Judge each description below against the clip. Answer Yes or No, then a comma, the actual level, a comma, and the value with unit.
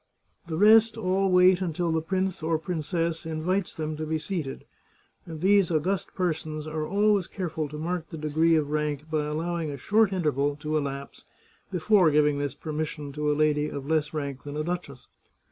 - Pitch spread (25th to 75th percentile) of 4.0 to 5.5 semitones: No, average, 3.2 semitones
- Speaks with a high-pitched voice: No, medium, 160 Hz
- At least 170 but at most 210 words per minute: Yes, average, 185 wpm